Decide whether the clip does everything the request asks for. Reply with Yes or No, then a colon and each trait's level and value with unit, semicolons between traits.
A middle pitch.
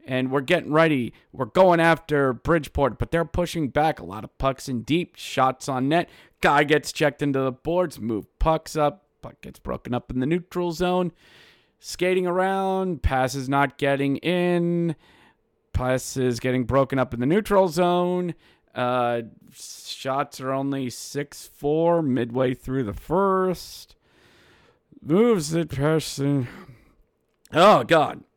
Yes: medium, 145 Hz